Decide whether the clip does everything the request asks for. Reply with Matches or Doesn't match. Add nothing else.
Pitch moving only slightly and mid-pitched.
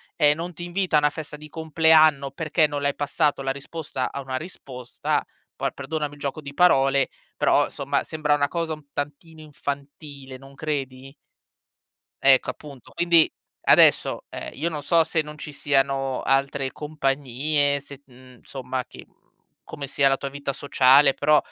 Matches